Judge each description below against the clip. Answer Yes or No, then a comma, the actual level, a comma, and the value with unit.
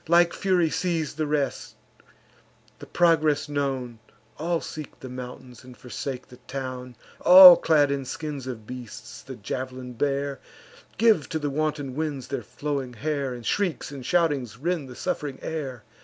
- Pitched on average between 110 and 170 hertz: Yes, medium, 140 Hz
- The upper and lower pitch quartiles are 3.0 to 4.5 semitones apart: Yes, average, 3.5 semitones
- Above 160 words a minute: No, average, 155 wpm